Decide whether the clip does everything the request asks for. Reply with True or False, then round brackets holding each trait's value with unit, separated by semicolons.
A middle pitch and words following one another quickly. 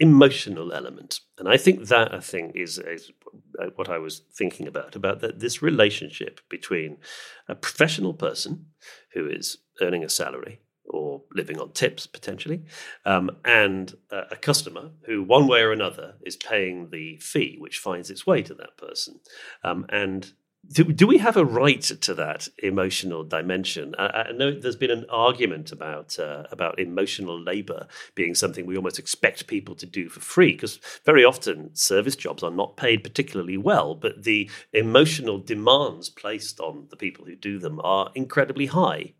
False (150 Hz; 170 wpm)